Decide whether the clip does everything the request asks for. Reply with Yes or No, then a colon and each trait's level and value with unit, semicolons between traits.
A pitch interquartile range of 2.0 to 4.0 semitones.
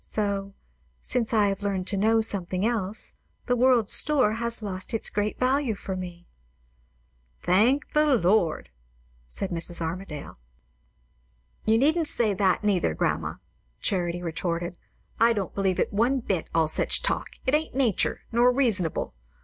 No: average, 4.4 semitones